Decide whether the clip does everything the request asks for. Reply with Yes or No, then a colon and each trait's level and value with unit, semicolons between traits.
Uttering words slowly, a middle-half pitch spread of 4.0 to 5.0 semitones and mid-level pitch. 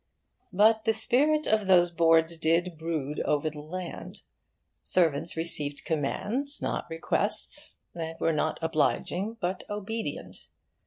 Yes: slow, 125 wpm; average, 4.5 semitones; medium, 170 Hz